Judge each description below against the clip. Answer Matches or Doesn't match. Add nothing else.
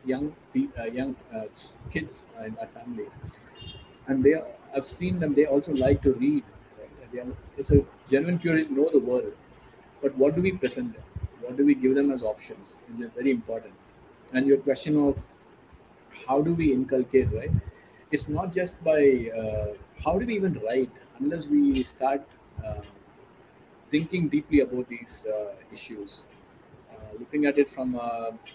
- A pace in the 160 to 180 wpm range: Matches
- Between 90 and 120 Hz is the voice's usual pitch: Doesn't match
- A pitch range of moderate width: Matches